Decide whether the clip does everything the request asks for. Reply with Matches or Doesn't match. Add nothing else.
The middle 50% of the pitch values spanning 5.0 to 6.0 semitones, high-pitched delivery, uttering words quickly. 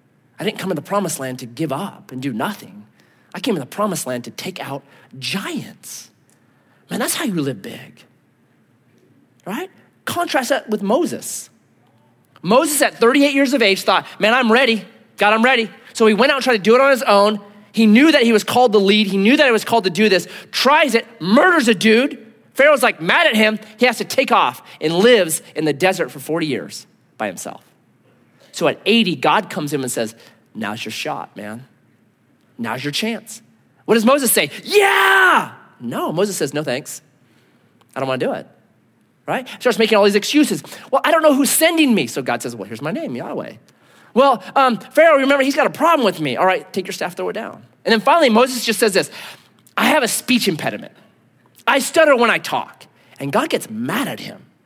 Matches